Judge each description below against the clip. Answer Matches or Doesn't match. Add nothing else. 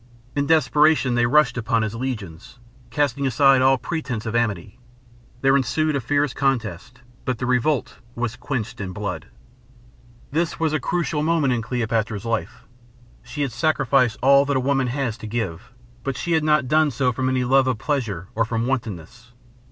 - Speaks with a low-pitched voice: Matches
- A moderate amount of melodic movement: Matches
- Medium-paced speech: Matches